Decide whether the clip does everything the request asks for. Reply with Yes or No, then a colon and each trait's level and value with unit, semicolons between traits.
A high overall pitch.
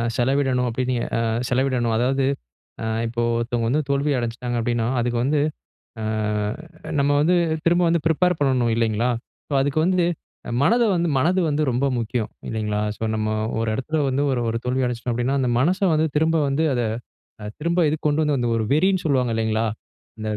No: low, 130 Hz